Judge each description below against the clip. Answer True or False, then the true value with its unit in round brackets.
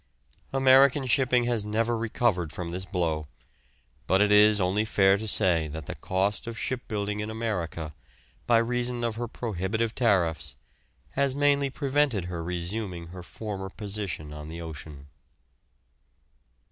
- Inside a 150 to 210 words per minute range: False (140 wpm)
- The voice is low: True (105 Hz)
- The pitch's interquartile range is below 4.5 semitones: False (5.1 semitones)